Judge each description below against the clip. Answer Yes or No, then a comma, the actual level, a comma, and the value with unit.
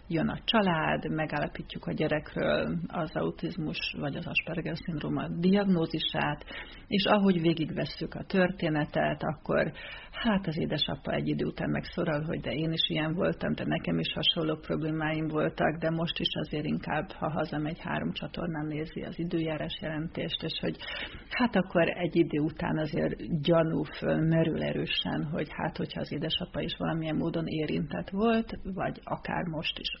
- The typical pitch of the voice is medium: Yes, medium, 165 Hz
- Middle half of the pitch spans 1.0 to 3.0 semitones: Yes, narrow, 2.4 semitones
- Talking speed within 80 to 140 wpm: No, fast, 155 wpm